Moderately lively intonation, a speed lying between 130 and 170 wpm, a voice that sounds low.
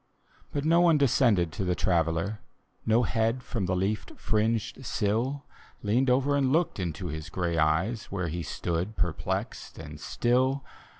No: wide, 6.7 semitones; average, 155 wpm; low, 105 Hz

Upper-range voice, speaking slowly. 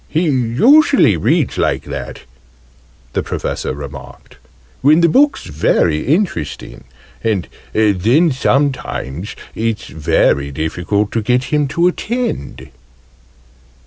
No: low, 115 Hz; slow, 105 wpm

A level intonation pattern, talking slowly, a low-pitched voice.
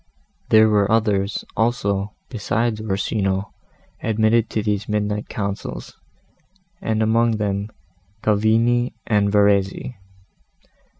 Yes: narrow, 1.7 semitones; slow, 95 wpm; low, 105 Hz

